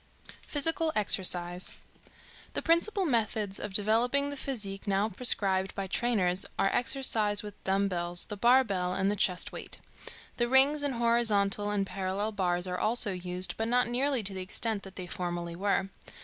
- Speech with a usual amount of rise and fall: Yes, average, 4.2 semitones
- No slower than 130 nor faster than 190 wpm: Yes, average, 165 wpm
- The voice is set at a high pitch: Yes, high, 205 Hz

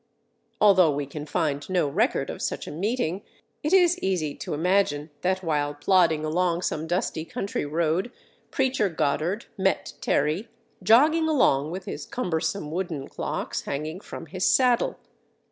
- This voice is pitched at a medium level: Yes, medium, 175 Hz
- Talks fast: No, average, 145 wpm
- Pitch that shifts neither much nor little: Yes, average, 4.6 semitones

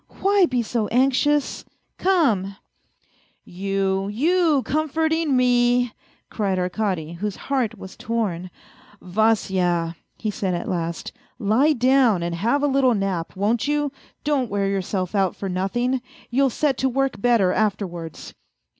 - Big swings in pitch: Yes, wide, 5.8 semitones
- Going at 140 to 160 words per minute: Yes, average, 155 wpm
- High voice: Yes, high, 220 Hz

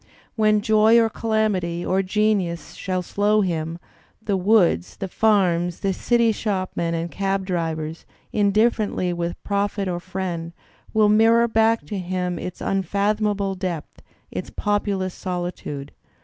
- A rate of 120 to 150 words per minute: Yes, slow, 135 wpm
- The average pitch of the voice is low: No, high, 195 Hz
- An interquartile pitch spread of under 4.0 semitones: Yes, average, 3.3 semitones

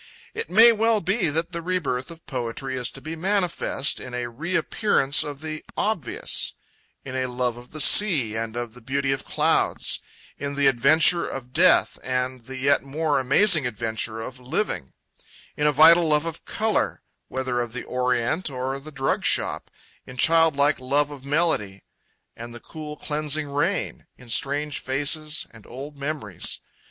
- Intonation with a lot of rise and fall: No, average, 3.9 semitones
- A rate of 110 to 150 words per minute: No, average, 165 wpm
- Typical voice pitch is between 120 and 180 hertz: Yes, medium, 140 Hz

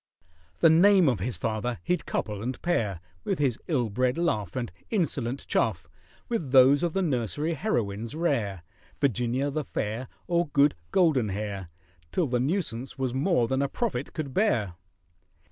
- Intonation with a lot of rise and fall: Yes, wide, 6.1 semitones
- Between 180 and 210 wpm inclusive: No, average, 155 wpm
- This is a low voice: Yes, low, 130 Hz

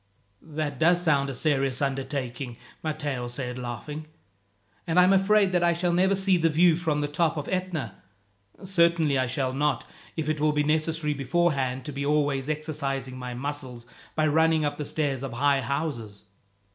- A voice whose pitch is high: No, medium, 150 Hz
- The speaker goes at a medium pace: Yes, average, 175 wpm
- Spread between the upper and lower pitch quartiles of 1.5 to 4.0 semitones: Yes, average, 3.2 semitones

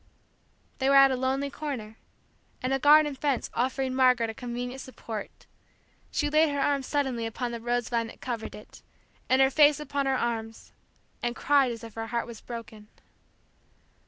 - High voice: Yes, very high, 255 Hz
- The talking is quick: No, average, 170 wpm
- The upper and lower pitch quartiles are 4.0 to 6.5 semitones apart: No, average, 2.9 semitones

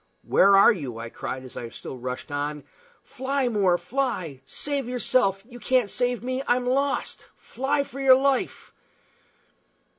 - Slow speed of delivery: No, average, 150 wpm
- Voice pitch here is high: Yes, high, 245 Hz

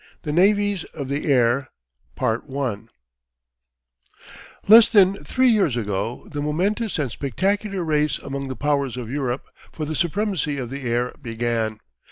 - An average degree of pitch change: No, wide, 7.2 semitones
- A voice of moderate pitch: Yes, medium, 145 Hz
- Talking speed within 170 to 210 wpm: No, slow, 135 wpm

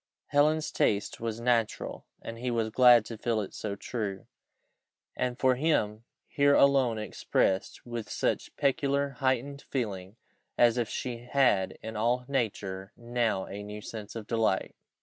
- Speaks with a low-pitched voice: Yes, low, 115 Hz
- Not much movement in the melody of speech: No, average, 3.2 semitones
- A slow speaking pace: No, average, 150 wpm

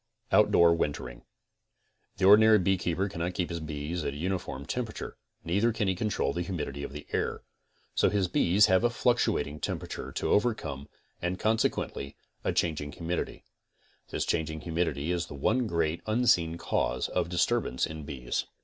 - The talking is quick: No, average, 160 wpm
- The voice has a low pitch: Yes, very low, 85 Hz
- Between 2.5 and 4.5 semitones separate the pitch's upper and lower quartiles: No, average, 5.1 semitones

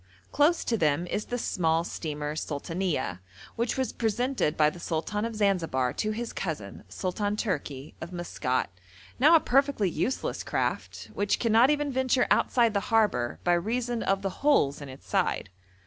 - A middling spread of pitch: No, wide, 7.4 semitones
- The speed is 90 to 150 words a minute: No, average, 165 wpm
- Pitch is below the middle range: No, high, 200 Hz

